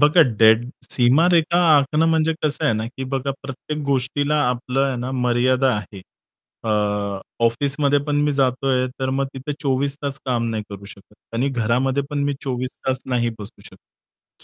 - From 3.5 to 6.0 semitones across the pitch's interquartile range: No, average, 2.7 semitones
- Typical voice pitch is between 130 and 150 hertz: Yes, low, 135 Hz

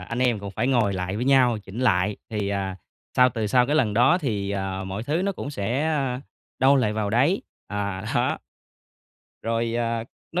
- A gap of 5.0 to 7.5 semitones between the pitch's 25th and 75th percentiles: No, average, 4.2 semitones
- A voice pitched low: Yes, low, 115 Hz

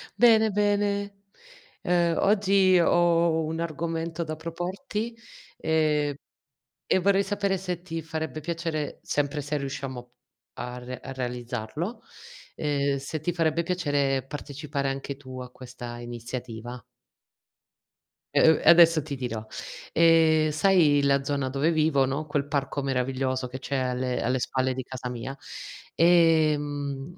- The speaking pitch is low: No, medium, 150 Hz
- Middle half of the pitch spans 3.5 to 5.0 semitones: Yes, average, 4.2 semitones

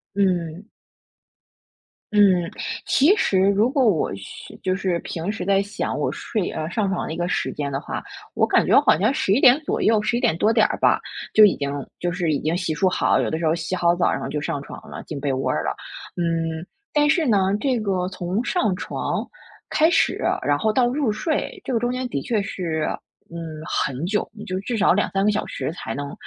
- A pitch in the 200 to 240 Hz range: No, high, 190 Hz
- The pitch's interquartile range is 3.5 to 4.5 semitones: No, average, 5.2 semitones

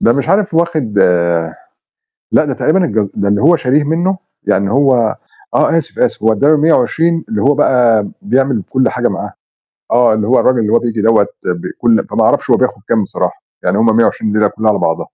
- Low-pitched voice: Yes, low, 125 Hz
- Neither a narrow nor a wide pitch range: No, wide, 5.9 semitones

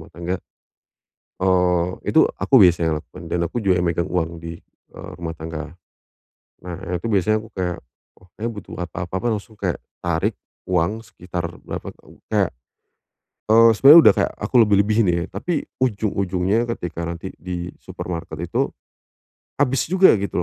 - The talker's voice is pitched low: Yes, very low, 90 Hz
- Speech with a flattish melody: No, average, 4.0 semitones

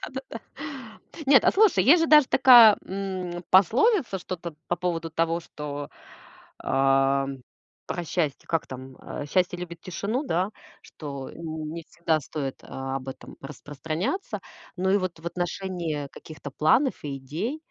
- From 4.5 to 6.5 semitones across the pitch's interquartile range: Yes, average, 5.0 semitones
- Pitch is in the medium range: Yes, medium, 170 Hz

